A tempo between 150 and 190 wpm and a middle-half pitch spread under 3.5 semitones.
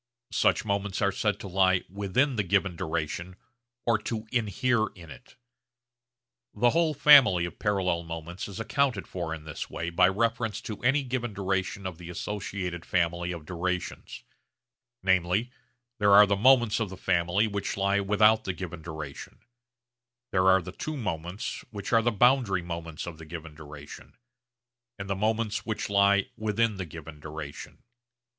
No: average, 160 wpm; average, 3.9 semitones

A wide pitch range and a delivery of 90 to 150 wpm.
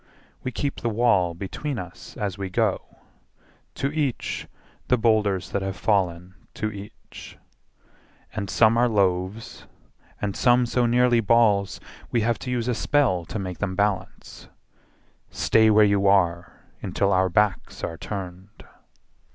No: average, 3.8 semitones; average, 145 wpm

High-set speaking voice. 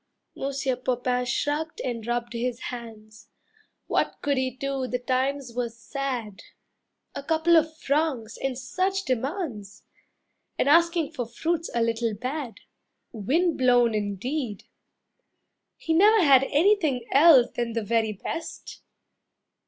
Yes: very high, 255 Hz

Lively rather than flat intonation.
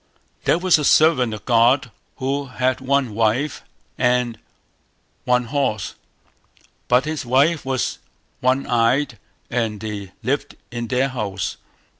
No: average, 3.1 semitones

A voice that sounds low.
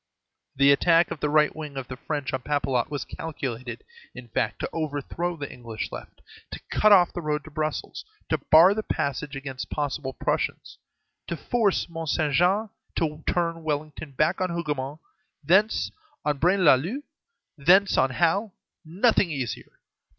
No: medium, 155 Hz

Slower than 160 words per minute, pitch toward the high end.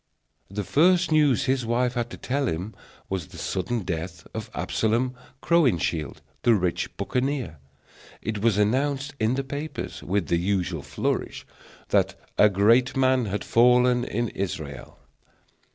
No: average, 140 wpm; low, 115 Hz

